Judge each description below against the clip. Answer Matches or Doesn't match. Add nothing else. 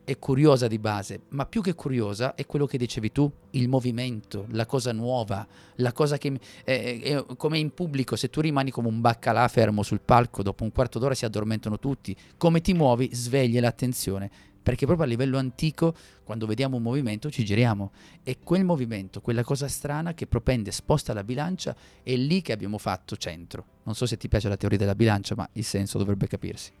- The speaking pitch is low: Matches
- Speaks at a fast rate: Matches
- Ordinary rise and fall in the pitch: Matches